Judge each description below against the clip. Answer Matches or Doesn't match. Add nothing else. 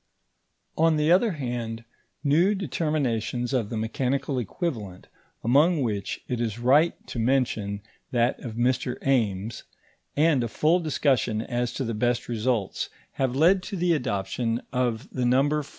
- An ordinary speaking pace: Matches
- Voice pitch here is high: Doesn't match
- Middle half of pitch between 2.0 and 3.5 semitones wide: Doesn't match